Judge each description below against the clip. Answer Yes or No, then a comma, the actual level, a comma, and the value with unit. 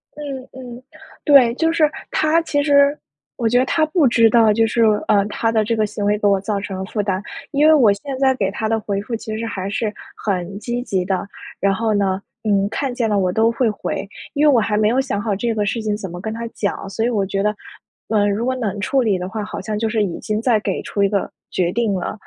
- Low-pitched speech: No, high, 220 Hz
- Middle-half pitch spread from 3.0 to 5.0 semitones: Yes, average, 3.3 semitones